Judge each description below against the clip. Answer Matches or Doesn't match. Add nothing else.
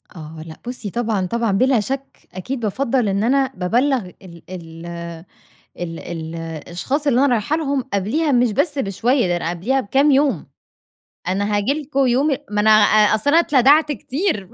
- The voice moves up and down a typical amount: Doesn't match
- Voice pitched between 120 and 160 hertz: Doesn't match